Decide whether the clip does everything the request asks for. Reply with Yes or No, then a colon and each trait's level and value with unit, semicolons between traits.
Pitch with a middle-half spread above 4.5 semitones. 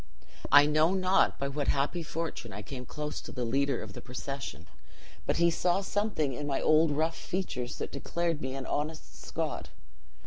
No: average, 3.6 semitones